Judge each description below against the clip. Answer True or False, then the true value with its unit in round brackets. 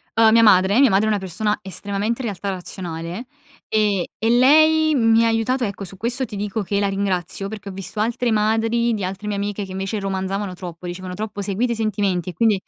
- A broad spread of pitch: False (2.9 semitones)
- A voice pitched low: False (205 Hz)